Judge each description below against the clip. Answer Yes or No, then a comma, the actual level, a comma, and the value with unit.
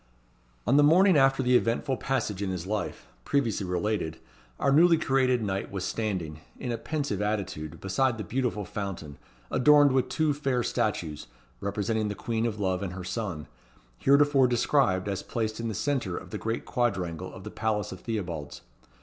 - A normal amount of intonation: No, wide, 5.9 semitones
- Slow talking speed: No, average, 175 wpm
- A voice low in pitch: Yes, low, 110 Hz